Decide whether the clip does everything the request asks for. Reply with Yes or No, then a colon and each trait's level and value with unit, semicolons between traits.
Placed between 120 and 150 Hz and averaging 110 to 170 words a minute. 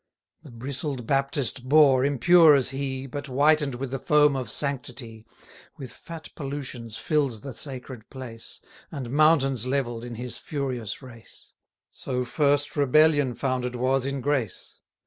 Yes: low, 135 Hz; average, 140 wpm